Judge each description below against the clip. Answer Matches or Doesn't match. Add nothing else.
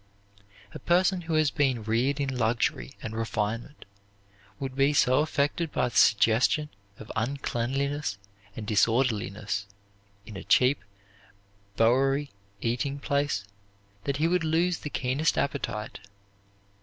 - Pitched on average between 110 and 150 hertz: Matches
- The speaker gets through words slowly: Matches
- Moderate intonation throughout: Matches